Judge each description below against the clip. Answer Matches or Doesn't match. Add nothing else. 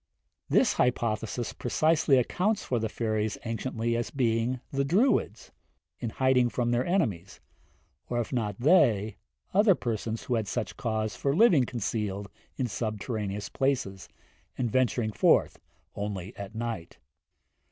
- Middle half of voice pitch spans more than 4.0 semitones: Doesn't match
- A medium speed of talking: Doesn't match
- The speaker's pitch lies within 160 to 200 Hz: Doesn't match